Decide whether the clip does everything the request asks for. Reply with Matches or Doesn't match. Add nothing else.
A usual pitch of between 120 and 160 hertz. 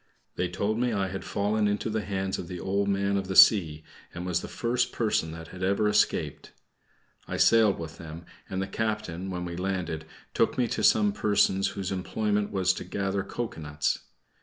Doesn't match